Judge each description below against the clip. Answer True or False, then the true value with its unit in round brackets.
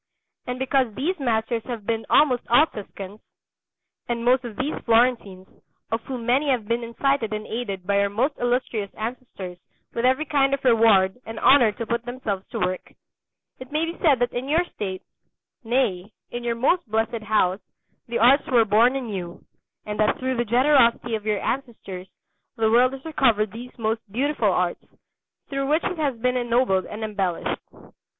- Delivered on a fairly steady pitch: False (3.4 semitones)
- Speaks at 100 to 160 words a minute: False (175 wpm)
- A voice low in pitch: False (235 Hz)